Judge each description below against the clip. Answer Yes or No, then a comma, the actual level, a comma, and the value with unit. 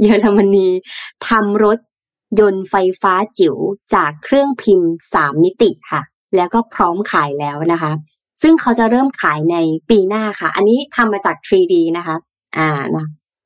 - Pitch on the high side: Yes, high, 195 Hz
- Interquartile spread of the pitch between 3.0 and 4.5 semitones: No, wide, 5.5 semitones